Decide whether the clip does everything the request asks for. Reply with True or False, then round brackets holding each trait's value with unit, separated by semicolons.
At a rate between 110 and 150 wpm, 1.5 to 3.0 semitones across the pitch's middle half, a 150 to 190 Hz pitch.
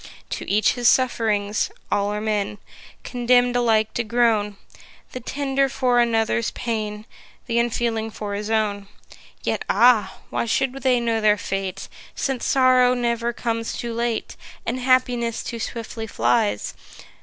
False (140 wpm; 2.5 semitones; 230 Hz)